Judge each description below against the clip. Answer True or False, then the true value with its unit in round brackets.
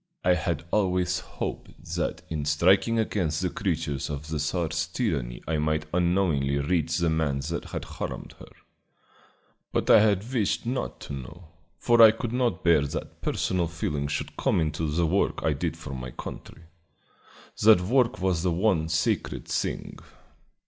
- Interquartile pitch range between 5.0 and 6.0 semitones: False (3.9 semitones)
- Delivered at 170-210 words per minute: False (160 wpm)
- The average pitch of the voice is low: True (85 Hz)